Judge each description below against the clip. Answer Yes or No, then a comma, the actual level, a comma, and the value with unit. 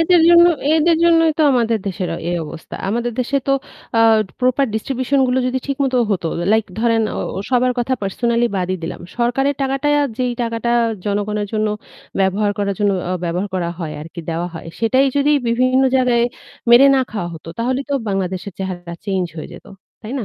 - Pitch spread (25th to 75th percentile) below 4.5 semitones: No, average, 5.3 semitones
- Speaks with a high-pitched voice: Yes, high, 230 Hz